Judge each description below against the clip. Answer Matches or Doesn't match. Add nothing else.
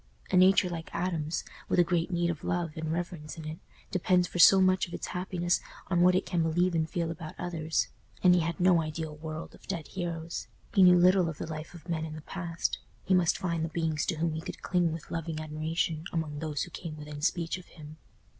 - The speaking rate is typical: Doesn't match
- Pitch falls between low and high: Matches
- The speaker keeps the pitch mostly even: Matches